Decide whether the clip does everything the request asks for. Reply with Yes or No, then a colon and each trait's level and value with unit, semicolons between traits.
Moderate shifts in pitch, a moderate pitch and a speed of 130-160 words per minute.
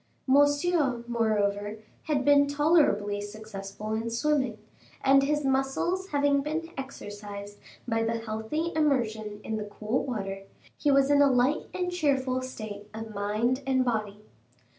No: average, 5.0 semitones; very high, 250 Hz; average, 140 wpm